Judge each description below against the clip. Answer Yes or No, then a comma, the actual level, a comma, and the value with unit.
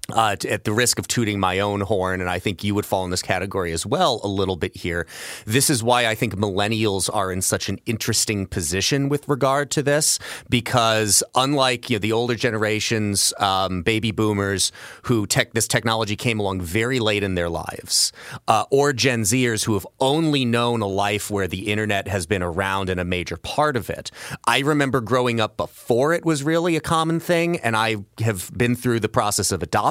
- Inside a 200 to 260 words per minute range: Yes, fast, 205 wpm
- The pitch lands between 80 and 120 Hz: Yes, low, 110 Hz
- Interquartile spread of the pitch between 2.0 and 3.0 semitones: No, average, 4.1 semitones